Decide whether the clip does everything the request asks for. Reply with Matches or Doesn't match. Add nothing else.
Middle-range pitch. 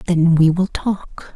Matches